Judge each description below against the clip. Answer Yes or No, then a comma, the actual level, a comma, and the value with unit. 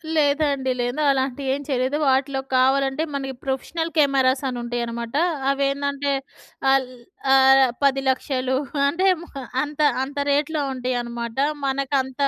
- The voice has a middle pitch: No, very high, 270 Hz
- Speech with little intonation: Yes, narrow, 1.5 semitones